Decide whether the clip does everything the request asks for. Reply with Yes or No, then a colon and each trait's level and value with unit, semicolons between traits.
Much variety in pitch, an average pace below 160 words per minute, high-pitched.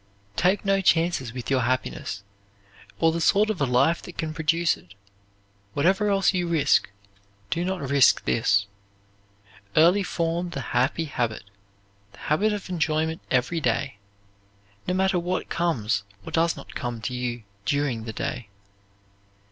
No: wide, 5.9 semitones; average, 150 wpm; medium, 160 Hz